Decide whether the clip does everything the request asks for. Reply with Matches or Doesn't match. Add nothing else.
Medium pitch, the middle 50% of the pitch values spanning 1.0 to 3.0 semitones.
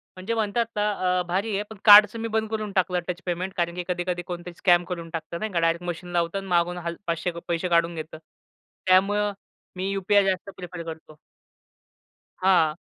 Matches